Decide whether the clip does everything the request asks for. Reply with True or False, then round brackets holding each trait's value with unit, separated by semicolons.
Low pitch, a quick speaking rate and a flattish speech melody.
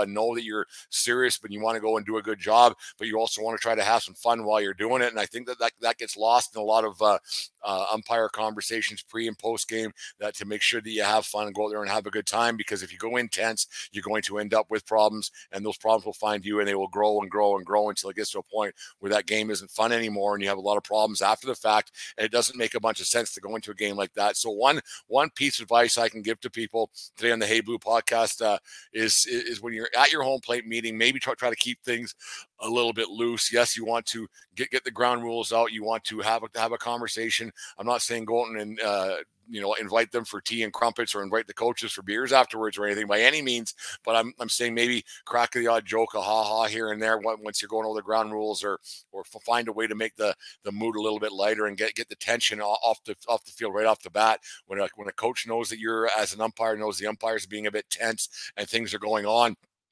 True (110 Hz; 285 wpm; 1.5 semitones)